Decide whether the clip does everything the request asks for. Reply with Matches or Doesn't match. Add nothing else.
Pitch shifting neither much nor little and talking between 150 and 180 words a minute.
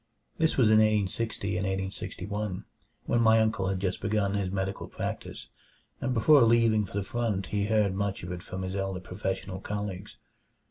Doesn't match